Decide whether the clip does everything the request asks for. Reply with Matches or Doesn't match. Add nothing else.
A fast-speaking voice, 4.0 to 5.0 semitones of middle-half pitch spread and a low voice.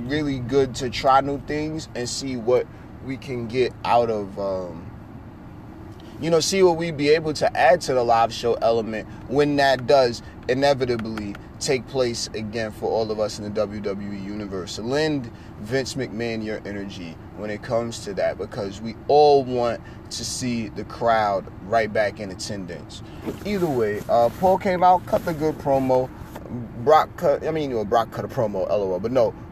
Doesn't match